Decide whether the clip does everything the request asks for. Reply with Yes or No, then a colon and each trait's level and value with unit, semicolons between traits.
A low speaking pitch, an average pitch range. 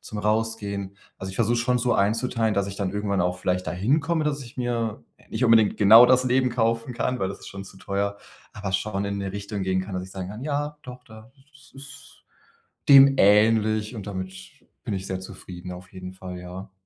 Yes: low, 105 Hz; average, 4.0 semitones